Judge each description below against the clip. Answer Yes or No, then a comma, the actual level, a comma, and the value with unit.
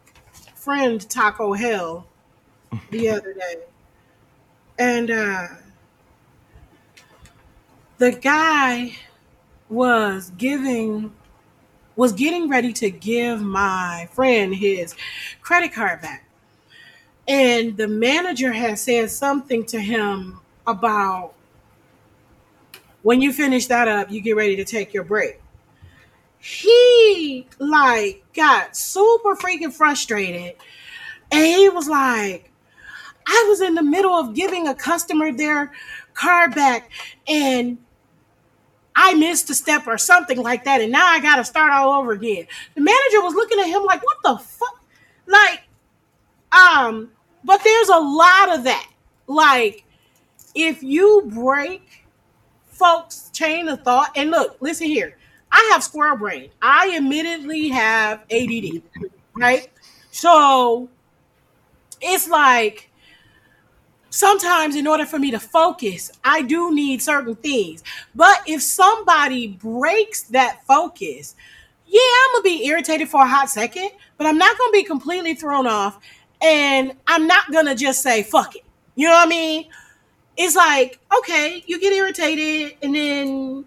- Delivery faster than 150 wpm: No, slow, 135 wpm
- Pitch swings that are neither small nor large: No, wide, 6.9 semitones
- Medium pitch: No, very high, 285 Hz